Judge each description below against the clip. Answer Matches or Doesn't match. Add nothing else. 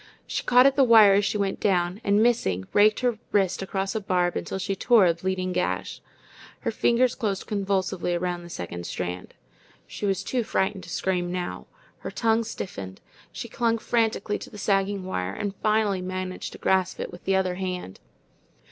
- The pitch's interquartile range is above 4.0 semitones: Doesn't match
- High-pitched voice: Matches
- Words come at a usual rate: Matches